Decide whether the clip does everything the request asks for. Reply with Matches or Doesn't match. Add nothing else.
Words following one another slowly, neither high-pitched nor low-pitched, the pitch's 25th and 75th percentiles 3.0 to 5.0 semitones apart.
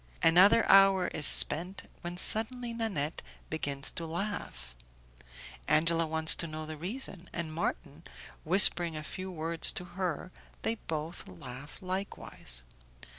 Matches